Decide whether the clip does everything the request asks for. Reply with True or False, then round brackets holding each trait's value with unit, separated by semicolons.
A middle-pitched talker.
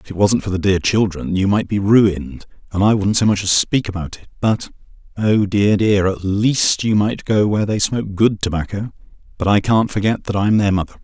False (100 Hz)